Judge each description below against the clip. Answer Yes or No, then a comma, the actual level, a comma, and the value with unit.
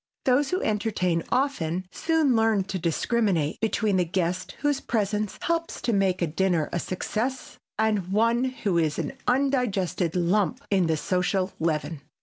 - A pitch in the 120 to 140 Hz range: No, high, 200 Hz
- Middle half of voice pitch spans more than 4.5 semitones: Yes, average, 5.0 semitones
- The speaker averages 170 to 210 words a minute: No, average, 150 wpm